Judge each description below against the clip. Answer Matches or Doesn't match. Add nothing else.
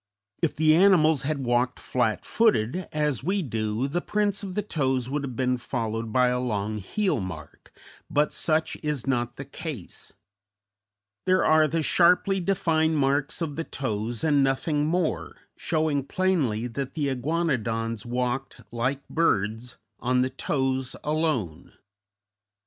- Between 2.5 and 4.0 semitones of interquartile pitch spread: Doesn't match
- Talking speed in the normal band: Matches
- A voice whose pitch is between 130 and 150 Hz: Matches